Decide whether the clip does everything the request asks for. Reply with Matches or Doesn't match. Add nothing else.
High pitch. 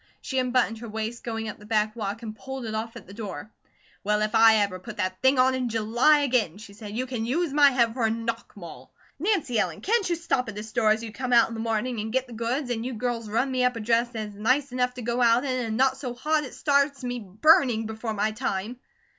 Matches